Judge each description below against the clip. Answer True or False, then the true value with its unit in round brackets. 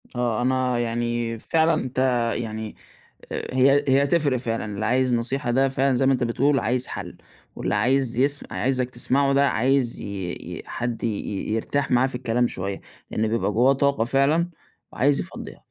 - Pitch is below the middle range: True (125 Hz)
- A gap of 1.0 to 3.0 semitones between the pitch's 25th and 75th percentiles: True (2.7 semitones)